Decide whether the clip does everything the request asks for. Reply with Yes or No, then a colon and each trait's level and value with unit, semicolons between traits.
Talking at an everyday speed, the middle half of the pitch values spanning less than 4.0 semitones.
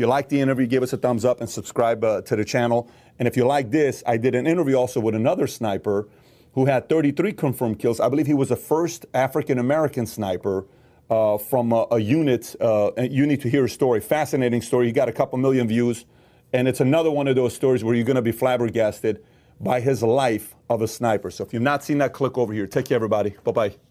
No: fast, 240 wpm; average, 2.9 semitones